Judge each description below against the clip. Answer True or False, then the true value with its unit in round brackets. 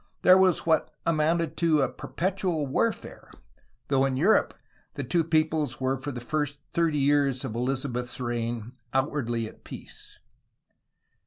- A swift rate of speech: False (140 wpm)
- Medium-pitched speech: True (145 Hz)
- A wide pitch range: False (4.2 semitones)